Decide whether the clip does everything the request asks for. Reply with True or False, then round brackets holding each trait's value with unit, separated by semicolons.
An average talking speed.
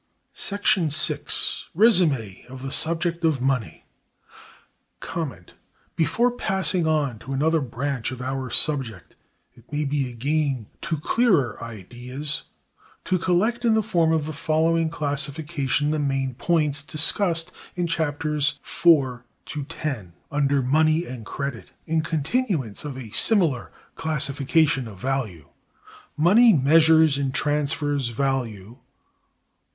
False (120 wpm)